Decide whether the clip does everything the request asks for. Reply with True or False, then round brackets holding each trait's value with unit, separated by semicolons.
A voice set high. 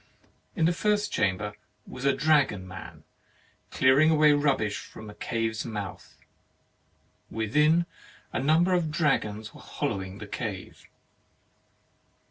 False (130 Hz)